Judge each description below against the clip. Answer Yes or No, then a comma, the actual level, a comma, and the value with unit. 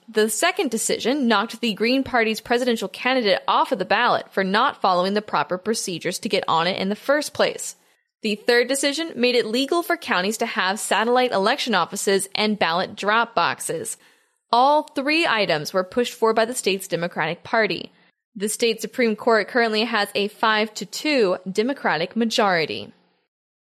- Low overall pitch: No, high, 225 Hz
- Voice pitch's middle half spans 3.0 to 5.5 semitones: Yes, average, 3.9 semitones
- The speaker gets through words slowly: No, average, 170 wpm